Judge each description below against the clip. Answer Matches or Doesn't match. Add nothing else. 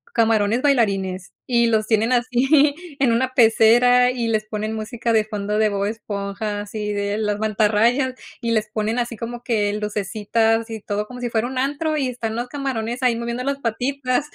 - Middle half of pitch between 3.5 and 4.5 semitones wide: Doesn't match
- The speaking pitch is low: Doesn't match